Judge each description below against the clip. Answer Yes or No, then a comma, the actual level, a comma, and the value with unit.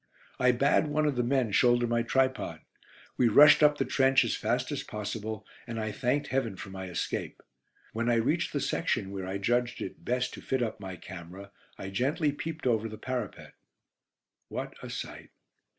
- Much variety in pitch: No, average, 4.1 semitones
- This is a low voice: Yes, low, 120 Hz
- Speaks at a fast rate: No, average, 185 wpm